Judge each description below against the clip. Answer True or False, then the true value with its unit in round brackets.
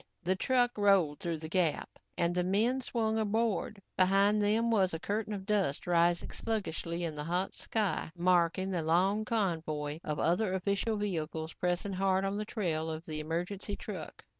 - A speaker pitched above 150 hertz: True (190 Hz)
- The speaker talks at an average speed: True (170 wpm)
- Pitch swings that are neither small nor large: True (3.7 semitones)